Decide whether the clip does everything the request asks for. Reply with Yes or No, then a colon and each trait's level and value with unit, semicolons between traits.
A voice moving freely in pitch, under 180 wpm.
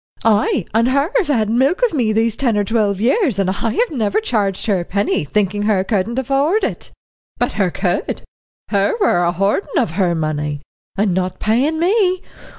No: wide, 5.9 semitones; average, 185 wpm